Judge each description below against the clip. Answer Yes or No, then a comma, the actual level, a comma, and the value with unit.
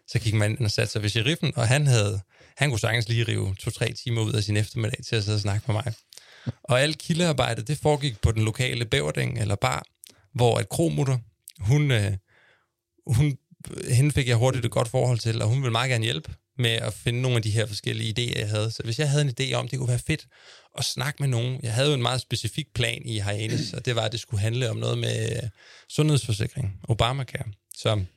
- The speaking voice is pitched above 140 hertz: No, low, 120 Hz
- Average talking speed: No, fast, 230 wpm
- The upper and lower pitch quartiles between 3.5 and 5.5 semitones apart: No, average, 3.1 semitones